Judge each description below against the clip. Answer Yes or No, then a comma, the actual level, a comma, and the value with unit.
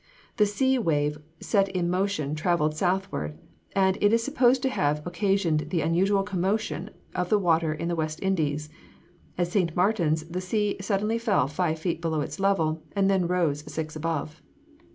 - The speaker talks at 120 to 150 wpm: No, average, 170 wpm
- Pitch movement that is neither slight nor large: Yes, average, 4.0 semitones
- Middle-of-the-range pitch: Yes, medium, 175 Hz